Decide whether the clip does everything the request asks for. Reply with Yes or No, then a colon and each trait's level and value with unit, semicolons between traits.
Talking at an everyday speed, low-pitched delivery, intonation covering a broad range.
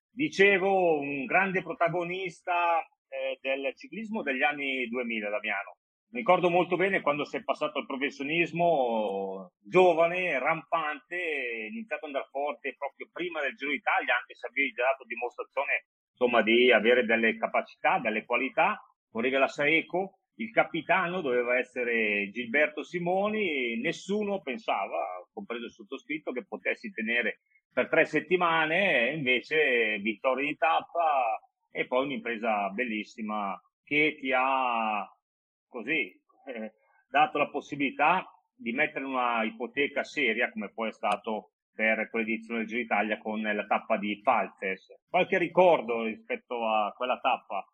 No: average, 135 wpm; medium, 145 Hz; wide, 6.7 semitones